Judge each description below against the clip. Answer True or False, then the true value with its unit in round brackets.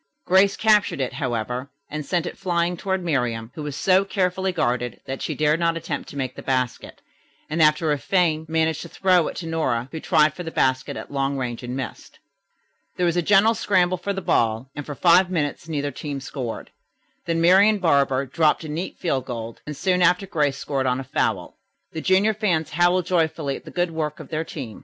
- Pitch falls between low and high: True (160 Hz)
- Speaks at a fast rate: True (210 wpm)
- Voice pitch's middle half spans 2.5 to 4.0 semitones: False (4.8 semitones)